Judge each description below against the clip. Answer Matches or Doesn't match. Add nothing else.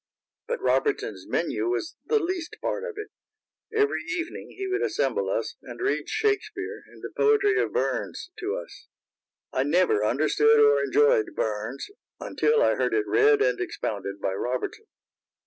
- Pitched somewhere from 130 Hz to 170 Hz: Doesn't match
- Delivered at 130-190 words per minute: Matches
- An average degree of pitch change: Matches